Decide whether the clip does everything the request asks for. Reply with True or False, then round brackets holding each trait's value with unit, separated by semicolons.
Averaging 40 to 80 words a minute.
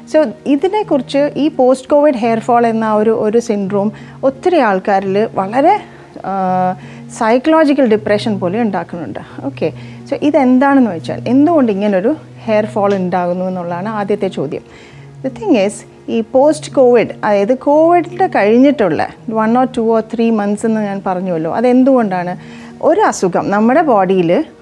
False (125 wpm)